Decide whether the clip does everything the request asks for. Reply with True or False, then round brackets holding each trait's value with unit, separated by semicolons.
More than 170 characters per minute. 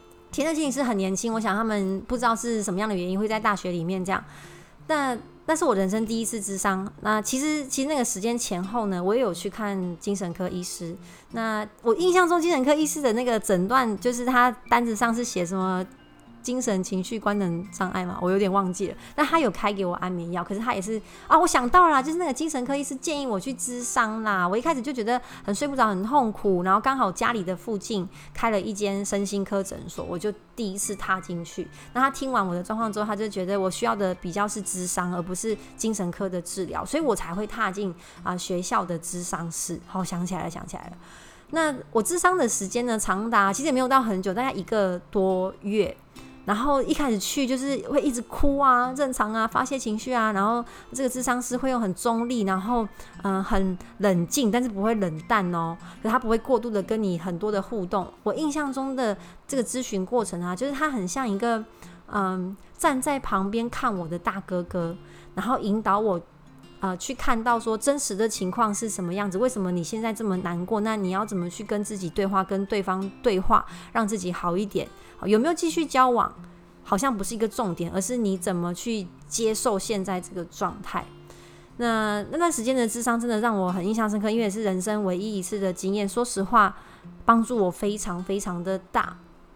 True (315 characters per minute)